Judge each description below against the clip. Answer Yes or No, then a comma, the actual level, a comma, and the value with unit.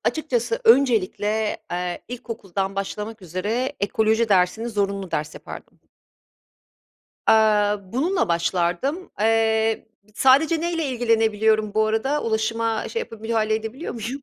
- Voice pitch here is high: Yes, high, 220 Hz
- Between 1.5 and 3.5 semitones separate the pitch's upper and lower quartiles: Yes, average, 3.0 semitones